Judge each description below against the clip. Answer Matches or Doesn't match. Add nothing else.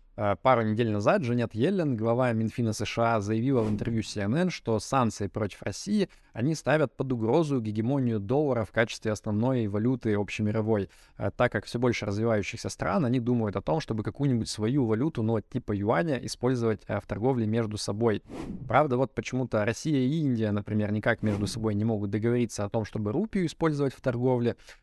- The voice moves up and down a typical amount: Matches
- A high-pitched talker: Doesn't match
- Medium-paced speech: Doesn't match